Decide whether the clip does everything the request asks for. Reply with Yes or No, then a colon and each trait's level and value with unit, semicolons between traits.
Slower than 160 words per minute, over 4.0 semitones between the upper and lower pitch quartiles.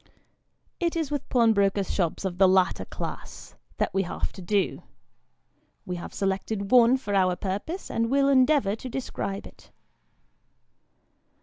Yes: average, 140 wpm; average, 5.2 semitones